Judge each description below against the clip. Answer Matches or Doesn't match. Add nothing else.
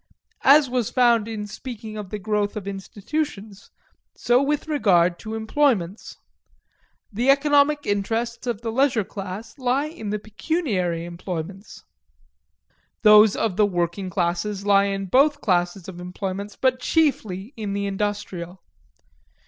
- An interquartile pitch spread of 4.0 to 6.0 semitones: Matches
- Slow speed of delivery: Matches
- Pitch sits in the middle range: Doesn't match